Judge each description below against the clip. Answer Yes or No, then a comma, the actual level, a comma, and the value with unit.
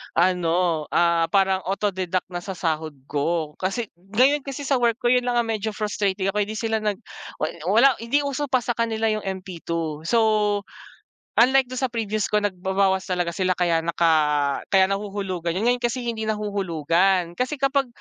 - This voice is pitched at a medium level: No, high, 200 Hz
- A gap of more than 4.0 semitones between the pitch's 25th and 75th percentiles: Yes, average, 4.9 semitones